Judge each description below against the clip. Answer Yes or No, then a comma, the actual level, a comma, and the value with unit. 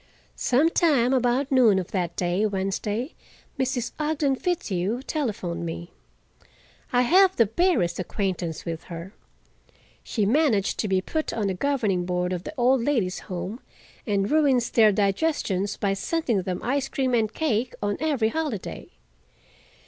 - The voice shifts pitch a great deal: Yes, wide, 6.2 semitones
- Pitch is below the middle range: No, high, 220 Hz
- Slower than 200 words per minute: Yes, average, 140 wpm